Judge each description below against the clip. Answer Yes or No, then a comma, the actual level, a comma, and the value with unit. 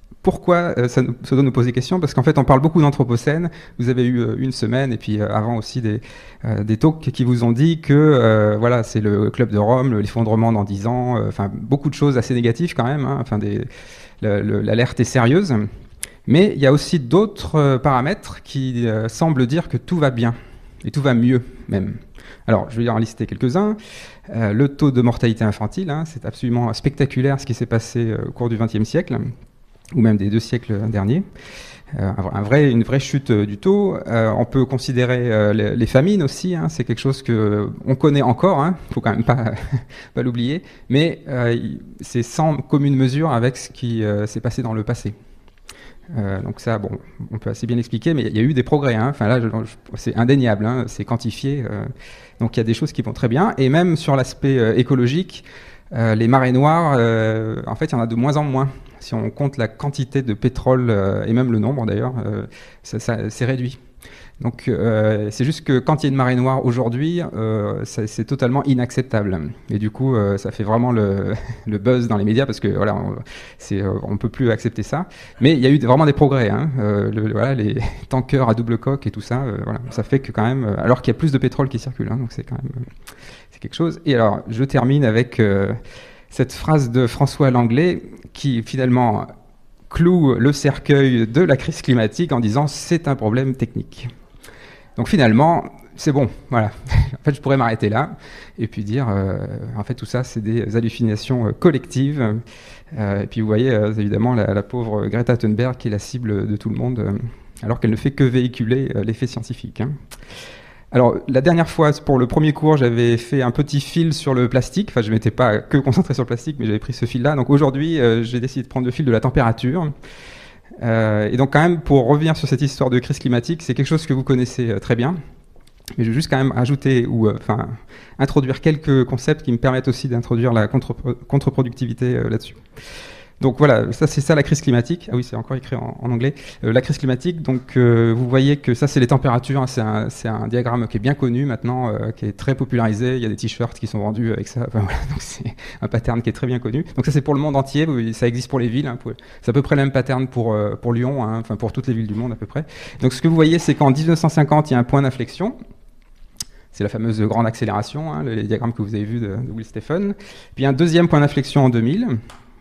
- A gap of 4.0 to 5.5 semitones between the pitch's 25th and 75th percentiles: No, average, 3.5 semitones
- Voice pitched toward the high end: No, low, 125 Hz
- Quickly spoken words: Yes, fast, 235 wpm